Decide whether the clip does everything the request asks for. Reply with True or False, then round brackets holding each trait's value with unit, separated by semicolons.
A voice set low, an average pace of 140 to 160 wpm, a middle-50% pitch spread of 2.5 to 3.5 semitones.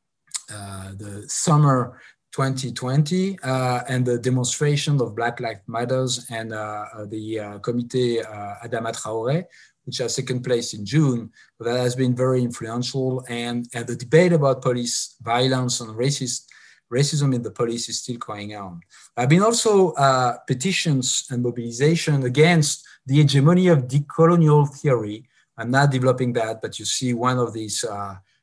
True (125 Hz; 150 wpm; 3.2 semitones)